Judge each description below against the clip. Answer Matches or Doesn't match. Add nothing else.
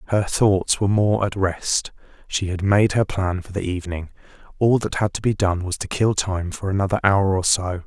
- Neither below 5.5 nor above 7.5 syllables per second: Doesn't match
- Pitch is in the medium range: Doesn't match